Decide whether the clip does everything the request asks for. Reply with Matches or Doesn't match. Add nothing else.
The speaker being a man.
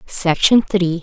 Doesn't match